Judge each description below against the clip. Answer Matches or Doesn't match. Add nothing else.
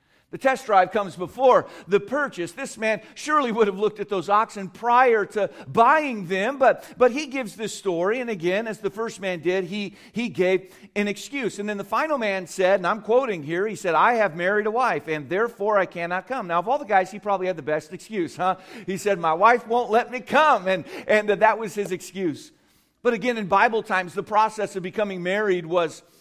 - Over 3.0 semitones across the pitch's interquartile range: Matches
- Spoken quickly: Matches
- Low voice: Doesn't match